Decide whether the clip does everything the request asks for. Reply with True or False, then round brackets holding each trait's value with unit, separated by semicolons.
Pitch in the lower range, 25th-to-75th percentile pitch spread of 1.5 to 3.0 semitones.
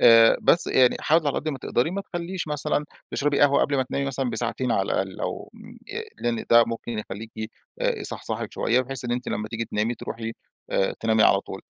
False (120 Hz; 3.8 semitones)